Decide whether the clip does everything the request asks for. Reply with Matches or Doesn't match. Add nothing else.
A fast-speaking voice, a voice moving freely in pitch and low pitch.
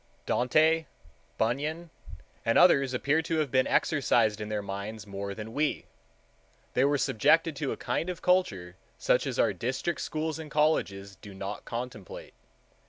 Doesn't match